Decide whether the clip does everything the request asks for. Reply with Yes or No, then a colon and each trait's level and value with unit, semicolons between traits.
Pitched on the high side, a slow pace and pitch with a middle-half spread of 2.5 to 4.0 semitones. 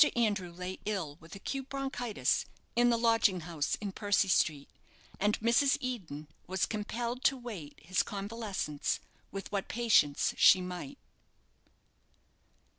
No: high, 200 Hz; slow, 125 wpm; average, 4.9 semitones